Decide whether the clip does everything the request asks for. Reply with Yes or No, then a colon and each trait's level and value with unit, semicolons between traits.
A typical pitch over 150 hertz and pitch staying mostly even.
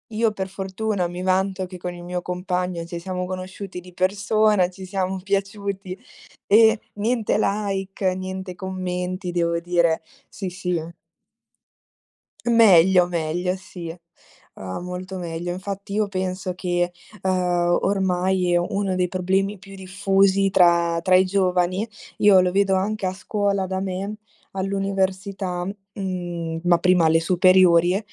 Yes: medium, 185 Hz; narrow, 1.6 semitones